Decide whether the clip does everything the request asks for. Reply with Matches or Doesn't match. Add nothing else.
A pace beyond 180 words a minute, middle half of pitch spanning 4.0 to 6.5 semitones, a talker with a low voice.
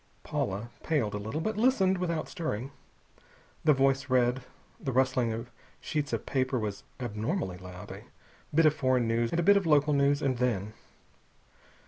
Doesn't match